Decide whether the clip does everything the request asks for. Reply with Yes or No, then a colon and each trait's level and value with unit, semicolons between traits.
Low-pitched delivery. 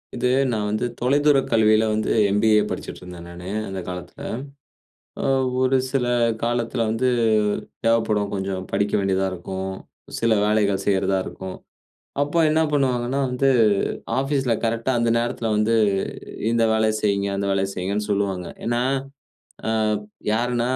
Yes: low, 110 Hz